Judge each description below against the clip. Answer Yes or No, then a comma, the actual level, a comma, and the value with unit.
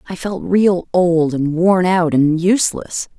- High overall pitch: No, medium, 175 Hz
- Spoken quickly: No, average, 170 wpm